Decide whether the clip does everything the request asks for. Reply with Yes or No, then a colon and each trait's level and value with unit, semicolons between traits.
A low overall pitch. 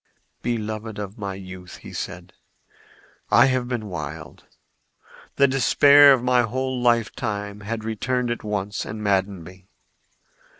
Yes: low, 110 Hz